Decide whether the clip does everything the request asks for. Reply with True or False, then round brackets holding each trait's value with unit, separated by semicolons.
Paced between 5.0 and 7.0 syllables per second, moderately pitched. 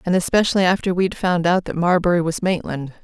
True (6.0 syllables/s; 175 Hz)